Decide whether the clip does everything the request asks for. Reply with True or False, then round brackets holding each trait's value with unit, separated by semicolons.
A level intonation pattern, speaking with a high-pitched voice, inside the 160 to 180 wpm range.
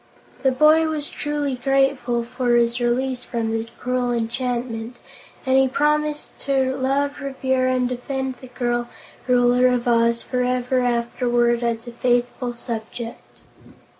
False (1.8 semitones; 250 Hz; 135 wpm)